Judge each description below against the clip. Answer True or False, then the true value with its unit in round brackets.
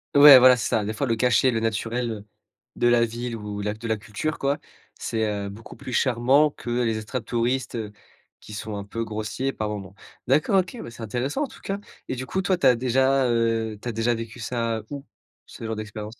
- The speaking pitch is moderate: False (115 Hz)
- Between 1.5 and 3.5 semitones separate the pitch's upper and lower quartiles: True (2.9 semitones)